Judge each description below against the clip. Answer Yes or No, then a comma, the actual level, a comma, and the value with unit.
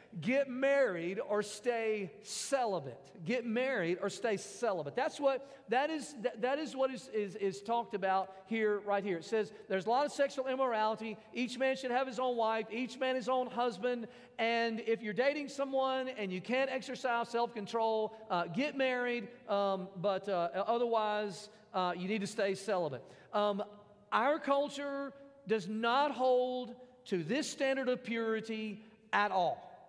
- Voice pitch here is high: Yes, high, 230 Hz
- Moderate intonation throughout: Yes, average, 3.8 semitones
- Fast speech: No, average, 165 wpm